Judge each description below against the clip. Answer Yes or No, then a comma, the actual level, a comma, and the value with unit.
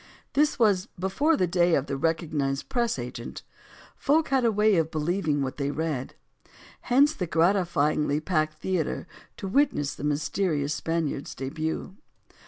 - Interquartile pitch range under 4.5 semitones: No, average, 5.2 semitones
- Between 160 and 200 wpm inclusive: No, average, 150 wpm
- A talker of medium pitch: Yes, medium, 165 Hz